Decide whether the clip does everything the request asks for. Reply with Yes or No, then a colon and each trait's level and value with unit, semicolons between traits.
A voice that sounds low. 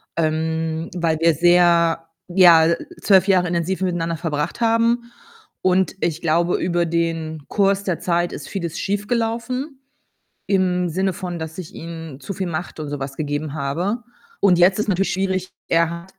No: medium, 175 Hz